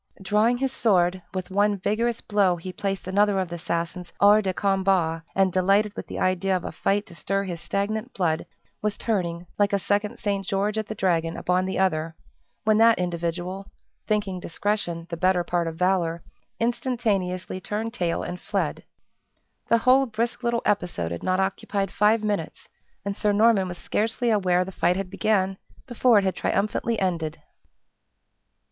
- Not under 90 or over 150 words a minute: No, average, 170 wpm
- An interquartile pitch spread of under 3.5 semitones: Yes, average, 2.9 semitones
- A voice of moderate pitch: No, high, 195 Hz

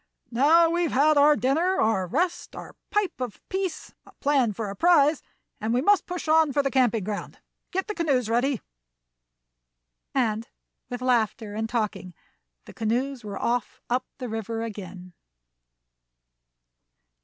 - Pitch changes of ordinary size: No, wide, 5.7 semitones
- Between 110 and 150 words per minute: Yes, average, 145 wpm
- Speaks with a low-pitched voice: No, very high, 255 Hz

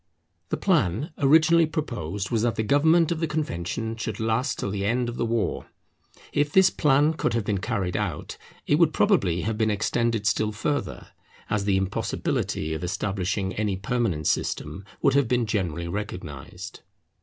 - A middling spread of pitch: No, wide, 6.5 semitones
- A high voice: No, low, 110 Hz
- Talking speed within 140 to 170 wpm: Yes, average, 165 wpm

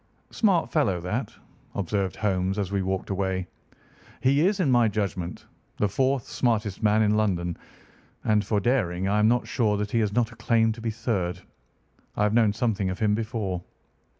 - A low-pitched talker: Yes, low, 105 Hz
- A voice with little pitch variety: No, average, 3.2 semitones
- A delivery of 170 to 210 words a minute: Yes, average, 180 wpm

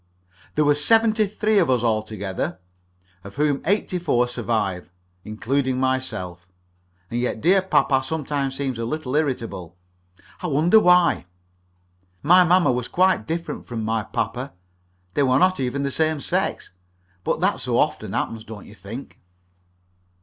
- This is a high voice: No, low, 135 Hz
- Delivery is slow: No, average, 150 wpm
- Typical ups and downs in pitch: No, wide, 6.3 semitones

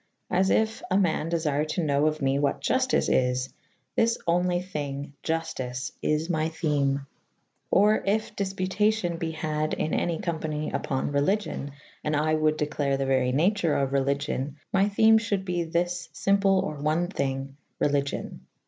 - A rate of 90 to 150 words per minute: No, average, 160 wpm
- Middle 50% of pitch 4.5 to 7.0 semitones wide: Yes, average, 4.8 semitones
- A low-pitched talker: No, medium, 155 Hz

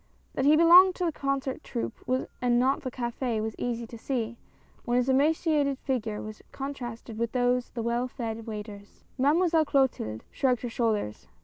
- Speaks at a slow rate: No, average, 185 wpm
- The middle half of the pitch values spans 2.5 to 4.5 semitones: Yes, average, 3.4 semitones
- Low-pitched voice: No, high, 245 Hz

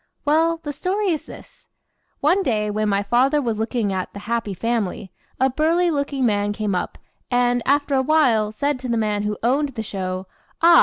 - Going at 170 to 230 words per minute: Yes, average, 195 wpm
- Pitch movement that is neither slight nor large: No, wide, 5.7 semitones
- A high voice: Yes, high, 245 Hz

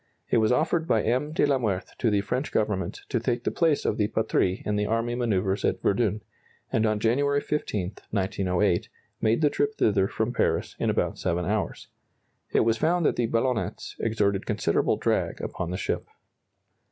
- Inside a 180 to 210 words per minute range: Yes, average, 185 wpm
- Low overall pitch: Yes, low, 110 Hz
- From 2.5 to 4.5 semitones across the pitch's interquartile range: Yes, average, 3.8 semitones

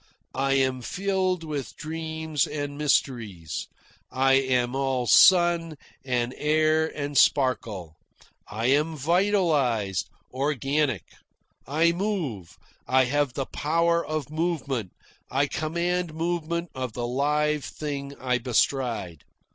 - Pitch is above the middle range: No, medium, 145 Hz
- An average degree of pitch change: Yes, average, 3.9 semitones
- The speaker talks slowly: Yes, slow, 110 wpm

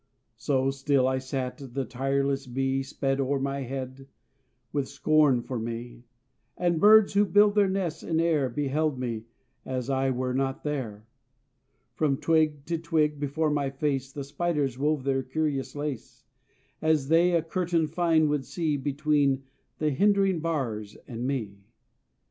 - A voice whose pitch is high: No, medium, 140 Hz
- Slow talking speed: No, average, 150 wpm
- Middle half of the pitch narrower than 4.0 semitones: Yes, average, 3.0 semitones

